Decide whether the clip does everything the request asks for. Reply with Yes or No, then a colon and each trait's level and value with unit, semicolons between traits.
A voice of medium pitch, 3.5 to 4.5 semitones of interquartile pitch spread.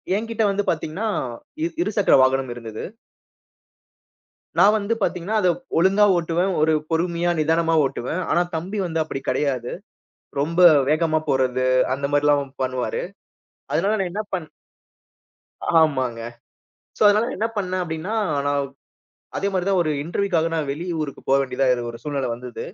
No: medium, 160 Hz; average, 5.2 semitones